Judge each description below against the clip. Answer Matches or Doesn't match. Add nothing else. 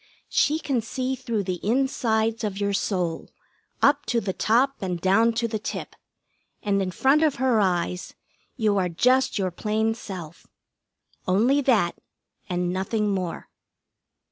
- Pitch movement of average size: Matches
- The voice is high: Matches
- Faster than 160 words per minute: Doesn't match